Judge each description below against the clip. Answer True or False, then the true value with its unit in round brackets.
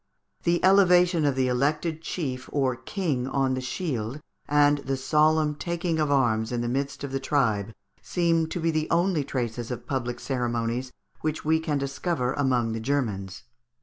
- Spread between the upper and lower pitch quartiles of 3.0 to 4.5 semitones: True (4.2 semitones)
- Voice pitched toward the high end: False (140 Hz)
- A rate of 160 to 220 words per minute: True (170 wpm)